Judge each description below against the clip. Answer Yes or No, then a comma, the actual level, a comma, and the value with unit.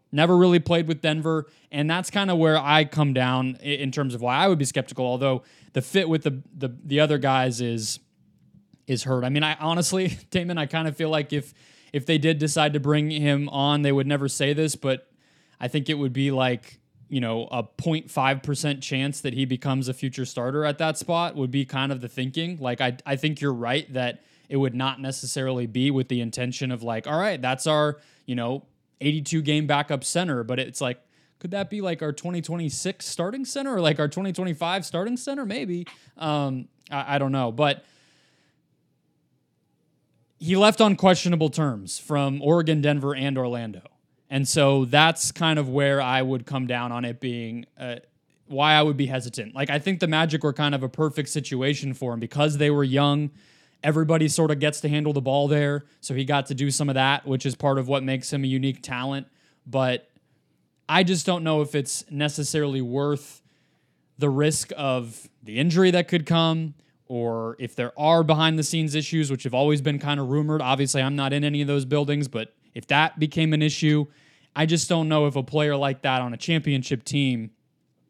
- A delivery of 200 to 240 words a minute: Yes, fast, 205 wpm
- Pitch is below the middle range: No, medium, 145 Hz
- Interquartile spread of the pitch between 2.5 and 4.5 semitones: Yes, average, 2.9 semitones